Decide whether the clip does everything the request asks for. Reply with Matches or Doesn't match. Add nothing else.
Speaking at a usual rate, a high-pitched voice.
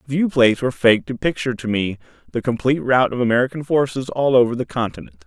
Doesn't match